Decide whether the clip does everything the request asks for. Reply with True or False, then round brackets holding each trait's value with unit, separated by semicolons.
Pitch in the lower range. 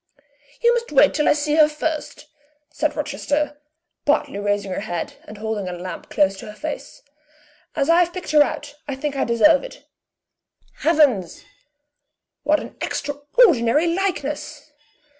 False (290 Hz)